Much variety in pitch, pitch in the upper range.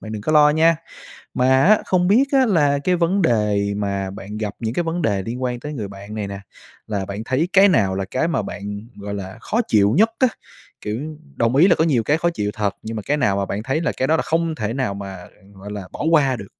No: wide, 7.8 semitones; low, 120 Hz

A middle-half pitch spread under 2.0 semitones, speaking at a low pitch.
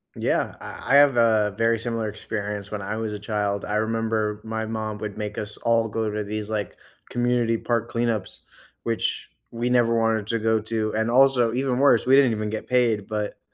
Yes: narrow, 1.6 semitones; low, 110 Hz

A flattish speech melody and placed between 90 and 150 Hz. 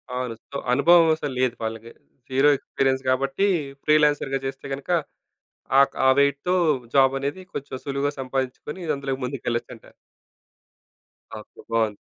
Yes: narrow, 1.8 semitones; low, 135 Hz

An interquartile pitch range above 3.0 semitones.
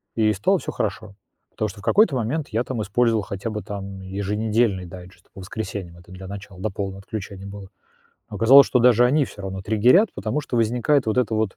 Yes: average, 3.5 semitones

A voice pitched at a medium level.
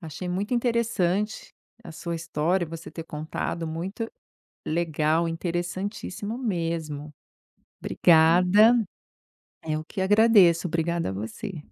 Yes: medium, 170 Hz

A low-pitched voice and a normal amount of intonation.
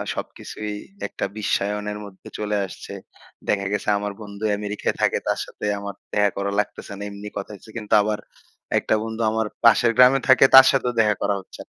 No: low, 105 Hz; narrow, 1.6 semitones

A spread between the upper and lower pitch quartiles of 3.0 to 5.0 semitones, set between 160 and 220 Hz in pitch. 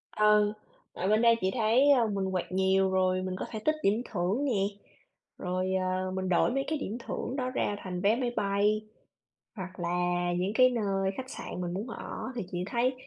Yes: average, 4.1 semitones; high, 200 Hz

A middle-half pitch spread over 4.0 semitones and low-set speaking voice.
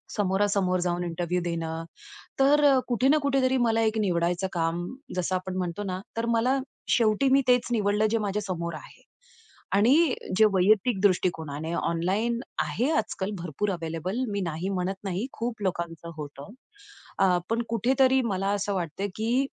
No: average, 4.7 semitones; high, 195 Hz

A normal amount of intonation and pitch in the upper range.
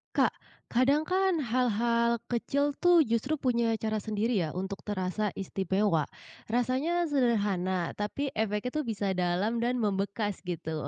Yes: average, 4.4 semitones; high, 225 Hz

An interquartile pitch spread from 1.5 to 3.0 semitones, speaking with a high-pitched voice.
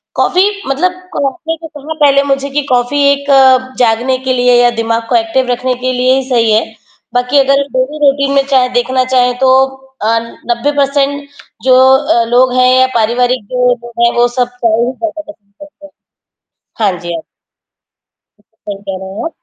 Yes: narrow, 2.6 semitones; very high, 255 Hz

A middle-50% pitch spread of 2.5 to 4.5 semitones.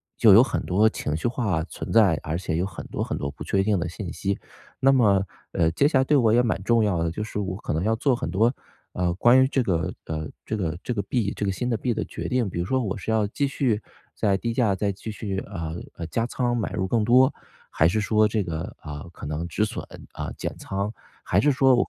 No: average, 4.9 semitones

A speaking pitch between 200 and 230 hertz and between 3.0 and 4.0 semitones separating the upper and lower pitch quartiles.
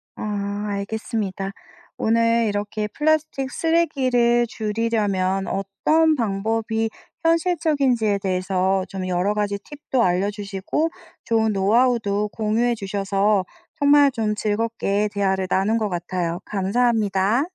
Yes: high, 210 Hz; average, 3.4 semitones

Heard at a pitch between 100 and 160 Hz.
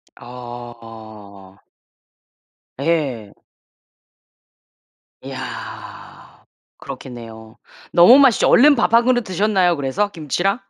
Yes: medium, 140 Hz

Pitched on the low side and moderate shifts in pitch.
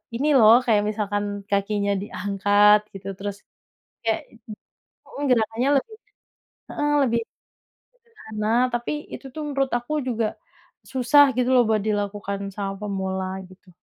No: high, 215 Hz; average, 3.1 semitones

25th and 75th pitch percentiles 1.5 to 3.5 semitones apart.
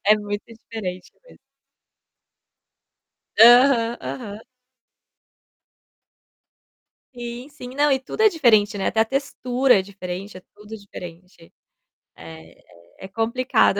No: average, 4.2 semitones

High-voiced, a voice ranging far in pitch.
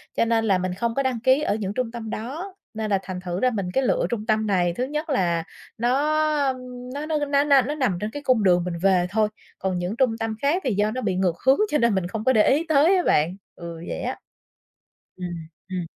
Yes: high, 220 Hz; wide, 5.9 semitones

